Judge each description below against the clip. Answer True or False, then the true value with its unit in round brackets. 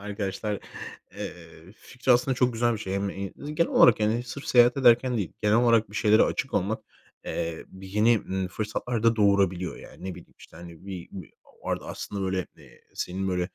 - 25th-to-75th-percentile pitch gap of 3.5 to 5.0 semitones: True (3.9 semitones)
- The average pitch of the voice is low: True (105 Hz)